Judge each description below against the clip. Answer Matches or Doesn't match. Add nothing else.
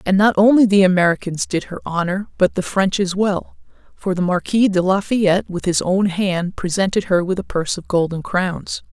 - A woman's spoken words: Matches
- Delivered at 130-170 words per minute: Doesn't match